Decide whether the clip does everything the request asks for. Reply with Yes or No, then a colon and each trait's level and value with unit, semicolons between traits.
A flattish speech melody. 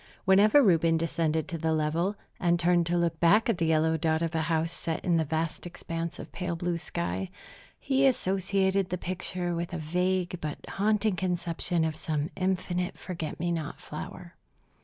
Yes: narrow, 2.3 semitones